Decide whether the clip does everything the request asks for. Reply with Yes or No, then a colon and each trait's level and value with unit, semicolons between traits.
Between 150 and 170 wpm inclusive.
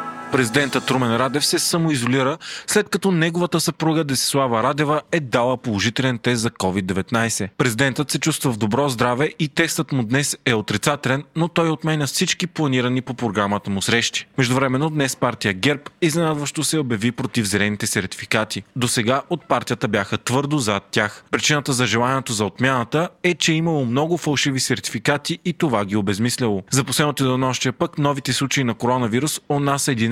Yes: fast, 165 wpm